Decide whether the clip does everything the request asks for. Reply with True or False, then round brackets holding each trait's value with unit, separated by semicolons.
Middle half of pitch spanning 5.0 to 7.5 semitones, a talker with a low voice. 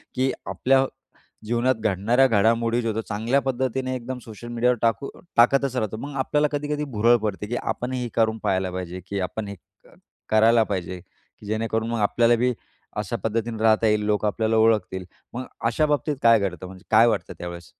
False (2.9 semitones; 115 Hz)